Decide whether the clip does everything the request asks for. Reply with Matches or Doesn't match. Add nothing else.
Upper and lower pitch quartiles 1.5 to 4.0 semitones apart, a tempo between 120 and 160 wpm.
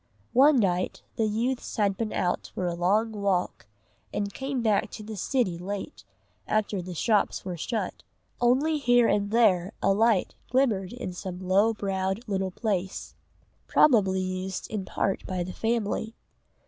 Matches